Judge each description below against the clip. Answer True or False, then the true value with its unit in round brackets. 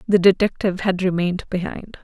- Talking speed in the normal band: True (150 wpm)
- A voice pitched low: False (185 Hz)